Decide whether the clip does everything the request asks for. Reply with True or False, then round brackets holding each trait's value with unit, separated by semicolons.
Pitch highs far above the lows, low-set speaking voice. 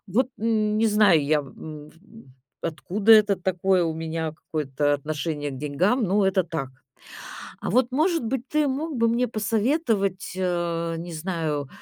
False (6.1 semitones; 185 Hz)